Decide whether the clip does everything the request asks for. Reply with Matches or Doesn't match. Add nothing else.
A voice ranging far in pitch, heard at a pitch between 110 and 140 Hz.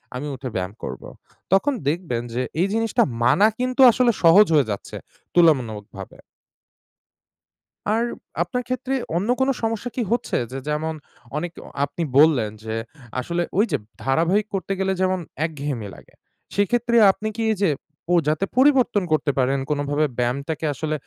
Doesn't match